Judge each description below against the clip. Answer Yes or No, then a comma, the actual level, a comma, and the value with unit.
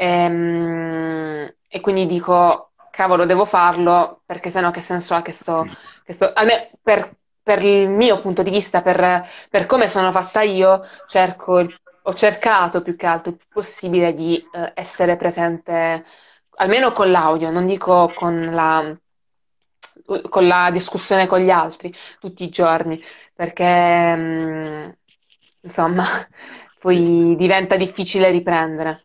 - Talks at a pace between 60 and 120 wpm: No, average, 130 wpm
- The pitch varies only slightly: Yes, narrow, 2.1 semitones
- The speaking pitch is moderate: Yes, medium, 180 Hz